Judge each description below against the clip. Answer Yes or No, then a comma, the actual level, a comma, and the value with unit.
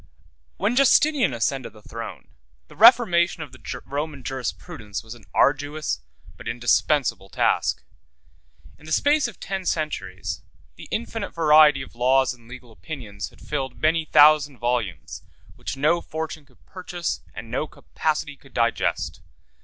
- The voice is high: No, medium, 145 Hz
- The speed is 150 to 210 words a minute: No, average, 140 wpm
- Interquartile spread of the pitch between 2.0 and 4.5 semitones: No, average, 5.1 semitones